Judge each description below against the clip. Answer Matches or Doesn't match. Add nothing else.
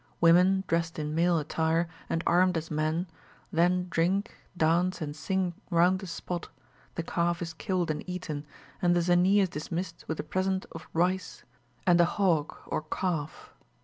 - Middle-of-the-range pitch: Matches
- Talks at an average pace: Matches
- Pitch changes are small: Matches